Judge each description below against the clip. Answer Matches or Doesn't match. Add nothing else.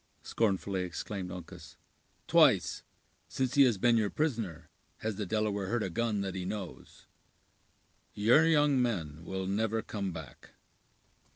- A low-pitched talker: Matches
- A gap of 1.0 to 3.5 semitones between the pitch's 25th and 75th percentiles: Doesn't match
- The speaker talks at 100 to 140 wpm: Matches